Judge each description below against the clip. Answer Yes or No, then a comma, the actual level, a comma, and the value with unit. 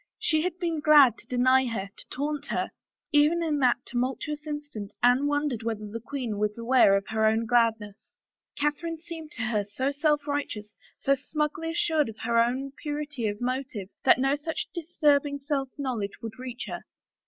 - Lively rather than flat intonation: No, average, 4.5 semitones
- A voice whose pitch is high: Yes, very high, 270 Hz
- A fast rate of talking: No, average, 175 wpm